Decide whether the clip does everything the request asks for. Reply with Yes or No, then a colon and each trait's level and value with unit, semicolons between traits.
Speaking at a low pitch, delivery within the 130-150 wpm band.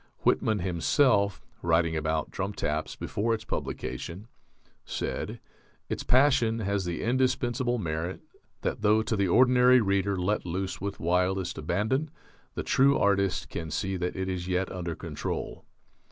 Yes: very low, 95 Hz; average, 140 wpm